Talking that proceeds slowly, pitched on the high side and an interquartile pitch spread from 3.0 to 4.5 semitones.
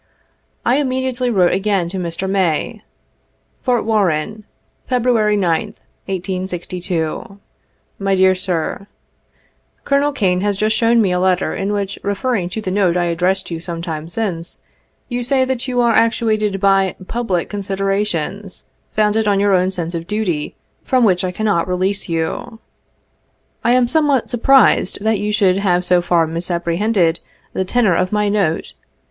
No: average, 160 wpm; high, 195 Hz; average, 3.5 semitones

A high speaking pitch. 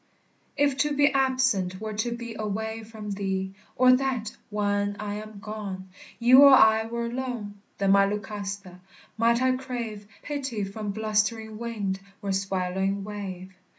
Yes: high, 215 Hz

